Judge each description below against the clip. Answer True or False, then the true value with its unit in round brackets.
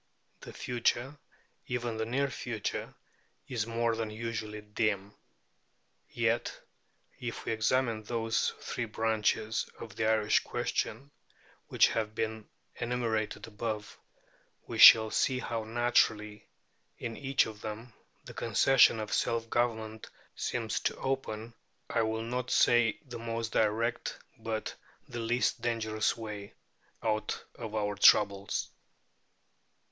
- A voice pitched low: True (115 Hz)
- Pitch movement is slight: True (1.6 semitones)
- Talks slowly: True (120 wpm)